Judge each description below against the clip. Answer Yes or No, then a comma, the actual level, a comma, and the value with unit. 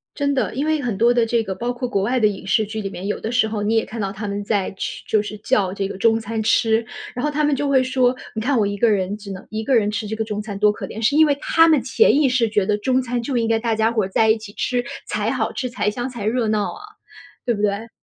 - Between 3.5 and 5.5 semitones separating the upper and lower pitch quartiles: No, average, 3.1 semitones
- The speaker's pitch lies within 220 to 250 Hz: Yes, high, 225 Hz